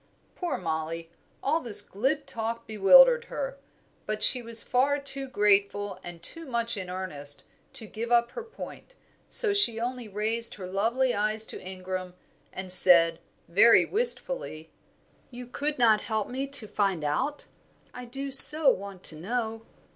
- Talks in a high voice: Yes, high, 225 Hz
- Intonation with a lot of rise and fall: Yes, wide, 6.1 semitones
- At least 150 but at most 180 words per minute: Yes, average, 155 wpm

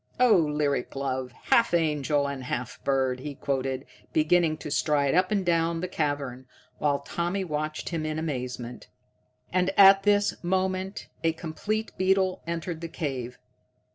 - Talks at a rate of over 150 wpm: No, average, 145 wpm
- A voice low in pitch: No, medium, 155 Hz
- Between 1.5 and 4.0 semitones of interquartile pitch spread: No, average, 4.7 semitones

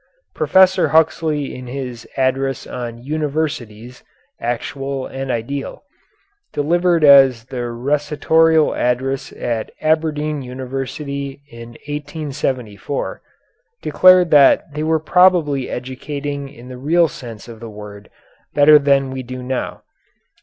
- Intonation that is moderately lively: Yes, average, 3.3 semitones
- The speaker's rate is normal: No, slow, 110 wpm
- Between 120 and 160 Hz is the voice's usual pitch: Yes, low, 135 Hz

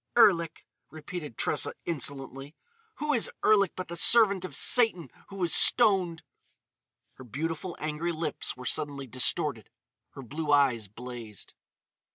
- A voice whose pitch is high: No, medium, 155 Hz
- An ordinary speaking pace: No, slow, 130 wpm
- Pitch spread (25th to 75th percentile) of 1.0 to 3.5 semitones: No, average, 5.2 semitones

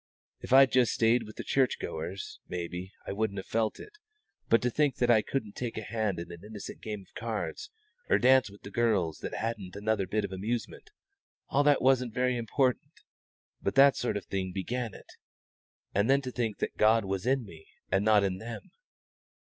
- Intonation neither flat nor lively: Yes, average, 4.1 semitones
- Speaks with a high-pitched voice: No, low, 110 Hz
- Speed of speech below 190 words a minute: No, fast, 205 wpm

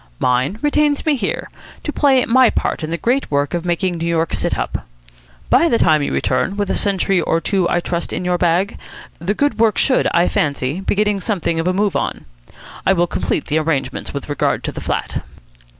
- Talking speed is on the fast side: Yes, fast, 215 wpm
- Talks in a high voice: No, medium, 180 Hz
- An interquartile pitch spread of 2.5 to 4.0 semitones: No, average, 4.4 semitones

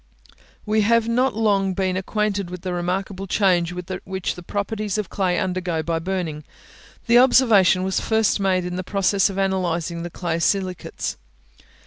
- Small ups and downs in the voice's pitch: Yes, narrow, 2.3 semitones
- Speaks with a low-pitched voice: No, high, 190 Hz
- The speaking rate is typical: Yes, average, 155 wpm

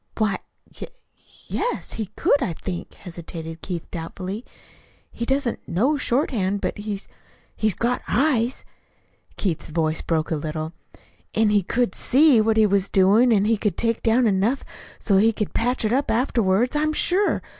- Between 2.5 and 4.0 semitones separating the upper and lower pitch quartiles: No, average, 4.7 semitones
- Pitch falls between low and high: No, high, 215 Hz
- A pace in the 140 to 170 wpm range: Yes, average, 165 wpm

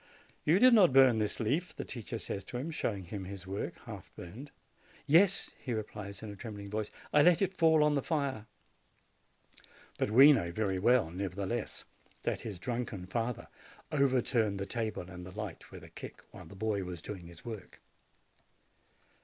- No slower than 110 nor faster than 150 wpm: No, average, 180 wpm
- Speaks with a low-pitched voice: Yes, low, 110 Hz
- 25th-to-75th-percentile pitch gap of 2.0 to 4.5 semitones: No, wide, 5.5 semitones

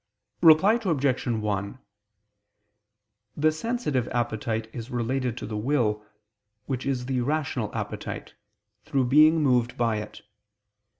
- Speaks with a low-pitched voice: Yes, low, 125 Hz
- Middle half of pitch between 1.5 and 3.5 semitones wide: No, average, 4.5 semitones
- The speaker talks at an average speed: No, slow, 115 wpm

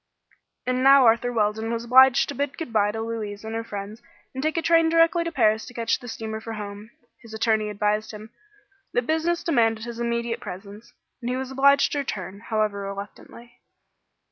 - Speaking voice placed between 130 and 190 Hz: No, high, 230 Hz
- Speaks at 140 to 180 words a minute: No, average, 195 wpm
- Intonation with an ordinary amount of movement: Yes, average, 3.5 semitones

